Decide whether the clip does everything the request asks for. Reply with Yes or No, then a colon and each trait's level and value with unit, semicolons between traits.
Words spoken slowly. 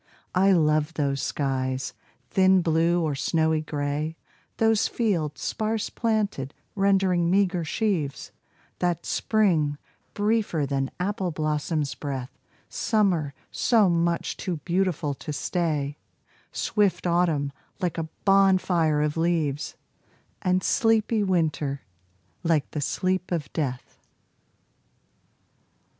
Yes: slow, 105 wpm